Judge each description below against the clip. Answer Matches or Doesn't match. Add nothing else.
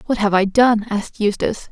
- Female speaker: Matches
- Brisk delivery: Matches